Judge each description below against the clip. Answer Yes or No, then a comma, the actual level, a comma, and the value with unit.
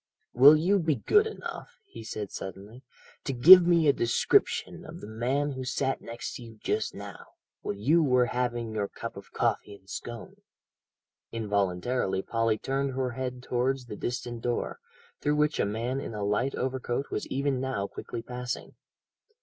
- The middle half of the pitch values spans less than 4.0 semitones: Yes, average, 3.4 semitones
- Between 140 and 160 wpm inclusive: No, average, 170 wpm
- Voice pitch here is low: Yes, low, 125 Hz